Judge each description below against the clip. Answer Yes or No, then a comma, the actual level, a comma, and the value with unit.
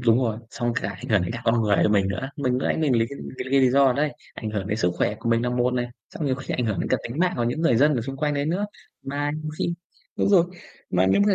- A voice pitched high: No, low, 125 Hz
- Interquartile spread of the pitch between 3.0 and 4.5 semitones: Yes, average, 4.0 semitones